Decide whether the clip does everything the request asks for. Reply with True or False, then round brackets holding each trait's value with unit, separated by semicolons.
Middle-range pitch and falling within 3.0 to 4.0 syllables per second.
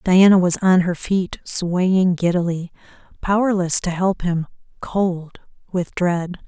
True (180 Hz; 3.7 syllables/s)